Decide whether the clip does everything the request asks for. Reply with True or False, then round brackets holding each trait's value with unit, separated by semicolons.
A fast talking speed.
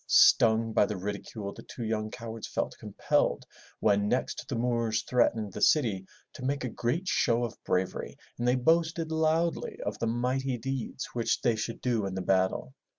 False (180 wpm)